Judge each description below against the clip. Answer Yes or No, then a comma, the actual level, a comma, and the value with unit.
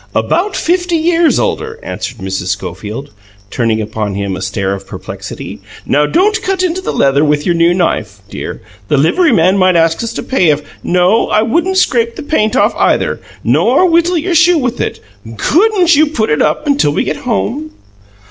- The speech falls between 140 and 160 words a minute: No, average, 185 wpm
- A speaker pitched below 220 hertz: No, high, 225 Hz